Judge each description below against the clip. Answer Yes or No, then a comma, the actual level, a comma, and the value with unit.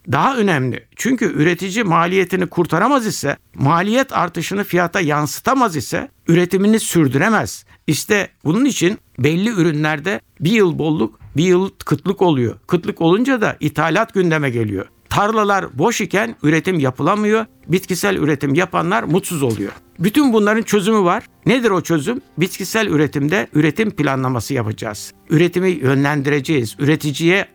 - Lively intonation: Yes, wide, 5.7 semitones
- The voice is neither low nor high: Yes, medium, 170 Hz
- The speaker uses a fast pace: No, average, 125 wpm